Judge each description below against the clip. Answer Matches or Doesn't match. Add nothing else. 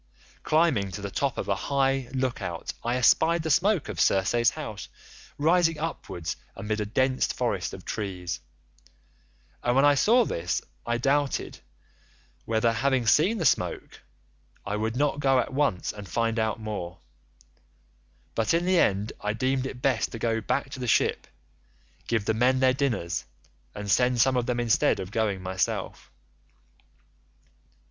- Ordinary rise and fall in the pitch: Matches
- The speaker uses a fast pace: Doesn't match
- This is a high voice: Doesn't match